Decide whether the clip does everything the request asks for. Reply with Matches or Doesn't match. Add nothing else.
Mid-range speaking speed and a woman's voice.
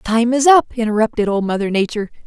Matches